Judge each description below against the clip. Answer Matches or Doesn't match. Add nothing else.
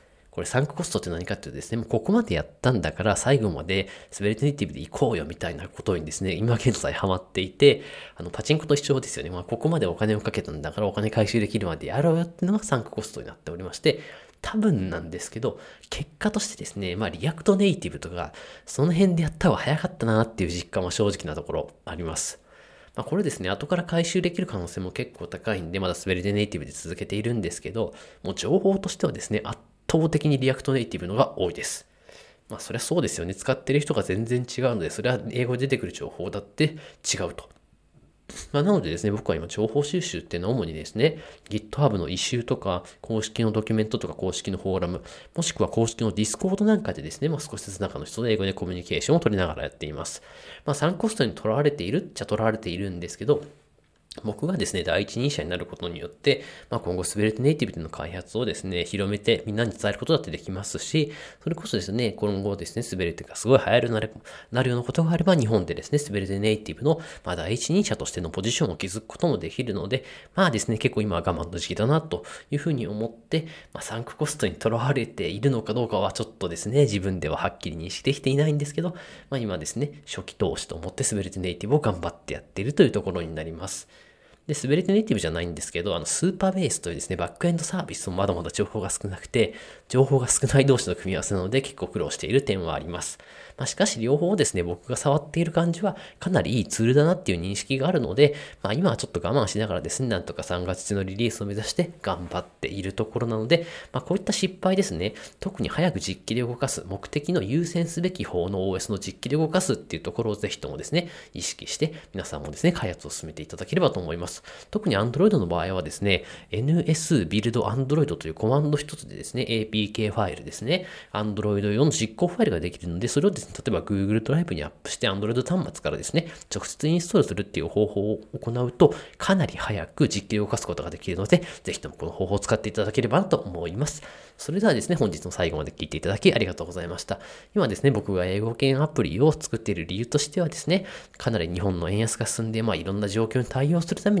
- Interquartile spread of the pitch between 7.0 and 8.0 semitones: Matches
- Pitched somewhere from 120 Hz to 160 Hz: Doesn't match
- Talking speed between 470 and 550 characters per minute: Matches